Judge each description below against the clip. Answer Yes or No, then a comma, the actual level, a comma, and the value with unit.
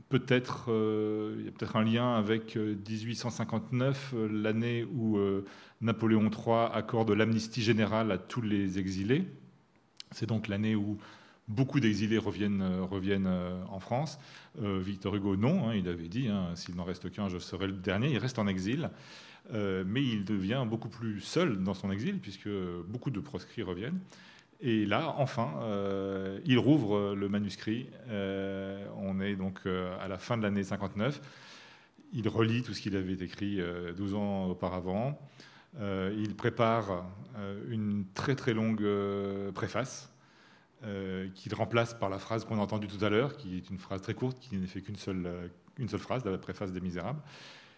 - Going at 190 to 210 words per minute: No, average, 180 wpm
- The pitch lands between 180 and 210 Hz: No, low, 105 Hz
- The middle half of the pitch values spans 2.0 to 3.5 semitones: Yes, average, 2.9 semitones